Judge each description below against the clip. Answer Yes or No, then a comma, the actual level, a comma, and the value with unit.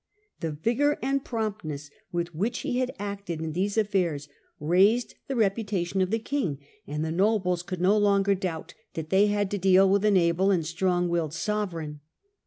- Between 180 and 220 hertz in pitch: Yes, high, 190 Hz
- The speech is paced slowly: No, average, 180 wpm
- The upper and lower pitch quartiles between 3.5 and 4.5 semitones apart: Yes, average, 3.8 semitones